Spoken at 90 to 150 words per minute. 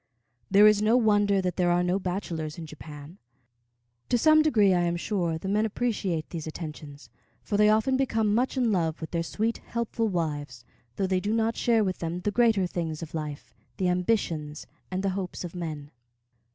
No: average, 190 wpm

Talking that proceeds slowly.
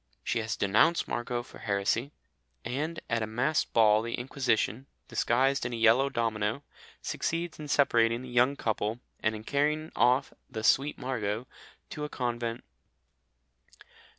No: average, 145 wpm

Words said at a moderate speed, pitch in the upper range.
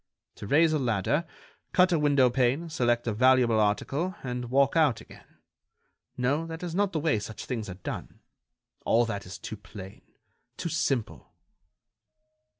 No: average, 150 wpm; low, 130 Hz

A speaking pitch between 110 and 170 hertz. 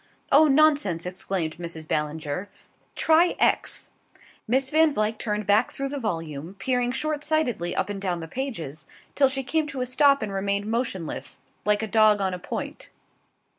No: high, 215 Hz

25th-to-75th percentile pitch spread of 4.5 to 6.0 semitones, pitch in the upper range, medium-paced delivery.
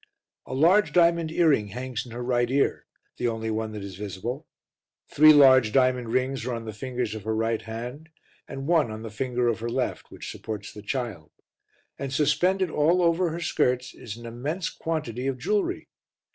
No: average, 4.9 semitones; low, 125 Hz; average, 185 wpm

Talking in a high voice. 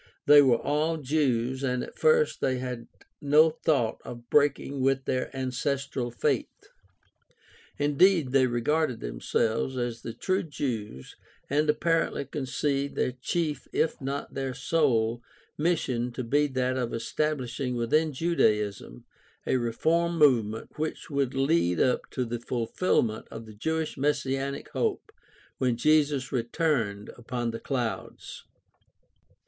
No: low, 130 Hz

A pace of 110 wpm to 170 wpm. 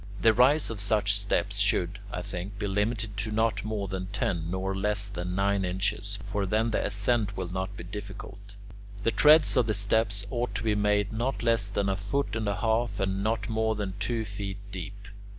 No: fast, 205 wpm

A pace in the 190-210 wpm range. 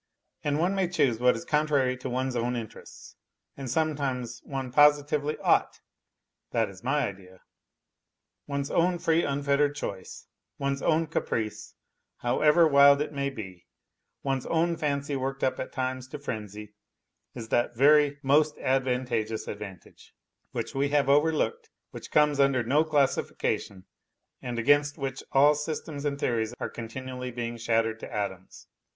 No: average, 150 wpm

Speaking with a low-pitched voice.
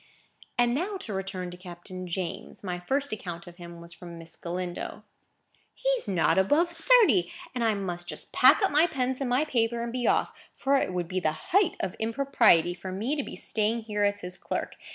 No: high, 205 Hz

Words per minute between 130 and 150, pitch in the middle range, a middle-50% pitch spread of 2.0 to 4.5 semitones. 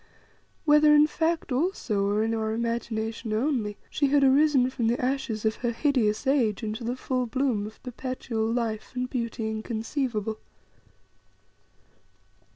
No: average, 140 wpm; high, 235 Hz; average, 3.5 semitones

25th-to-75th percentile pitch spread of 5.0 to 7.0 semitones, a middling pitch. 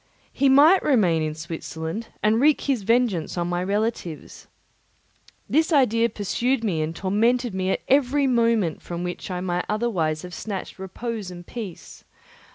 No: wide, 5.4 semitones; high, 210 Hz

